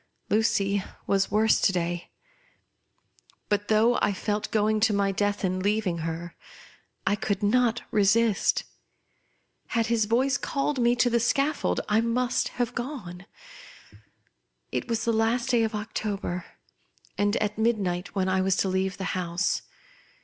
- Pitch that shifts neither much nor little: Yes, average, 3.2 semitones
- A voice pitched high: Yes, high, 210 Hz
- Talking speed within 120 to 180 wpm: Yes, average, 145 wpm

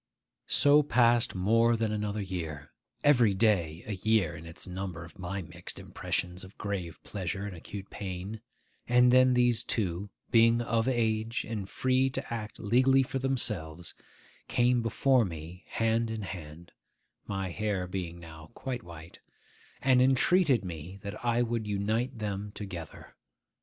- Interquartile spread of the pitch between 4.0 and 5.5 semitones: Yes, average, 4.7 semitones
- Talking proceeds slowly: No, average, 145 wpm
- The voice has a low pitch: Yes, low, 105 Hz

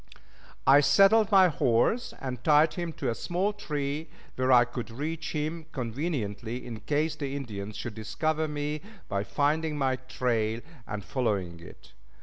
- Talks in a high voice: No, medium, 140 Hz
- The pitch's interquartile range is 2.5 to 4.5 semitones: No, average, 5.3 semitones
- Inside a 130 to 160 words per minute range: Yes, average, 155 wpm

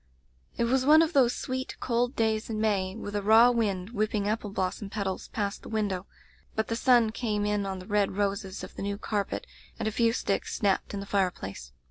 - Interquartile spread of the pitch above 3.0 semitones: No, narrow, 2.5 semitones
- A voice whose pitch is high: Yes, high, 210 Hz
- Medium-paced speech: No, fast, 215 wpm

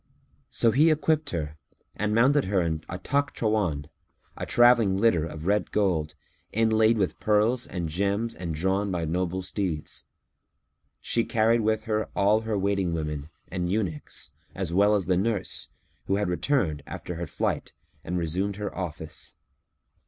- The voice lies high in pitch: No, low, 100 Hz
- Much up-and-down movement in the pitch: No, average, 4.2 semitones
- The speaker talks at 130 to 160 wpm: Yes, average, 150 wpm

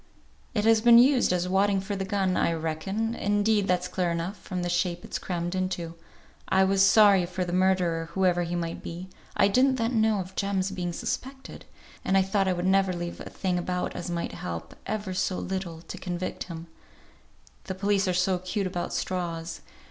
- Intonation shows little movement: Yes, narrow, 2.1 semitones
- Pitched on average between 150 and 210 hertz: Yes, medium, 185 Hz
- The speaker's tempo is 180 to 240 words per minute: Yes, average, 200 wpm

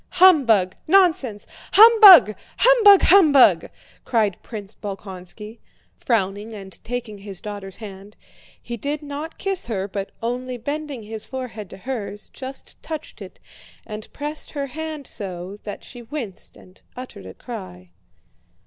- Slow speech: Yes, slow, 130 wpm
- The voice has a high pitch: Yes, high, 230 Hz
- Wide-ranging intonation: Yes, wide, 6.4 semitones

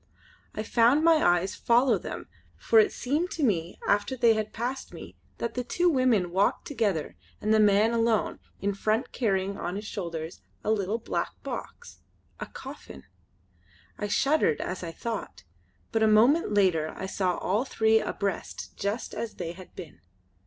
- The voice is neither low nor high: No, high, 215 Hz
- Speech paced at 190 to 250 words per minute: No, average, 165 wpm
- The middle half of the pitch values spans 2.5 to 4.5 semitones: Yes, average, 3.9 semitones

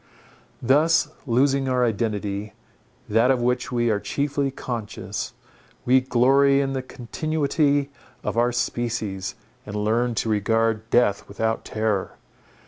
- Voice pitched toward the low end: Yes, low, 120 Hz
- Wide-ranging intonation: No, average, 3.5 semitones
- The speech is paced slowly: Yes, slow, 125 wpm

